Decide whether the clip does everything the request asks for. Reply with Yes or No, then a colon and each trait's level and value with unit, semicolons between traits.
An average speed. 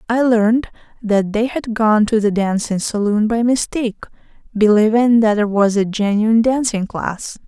Yes: average, 160 wpm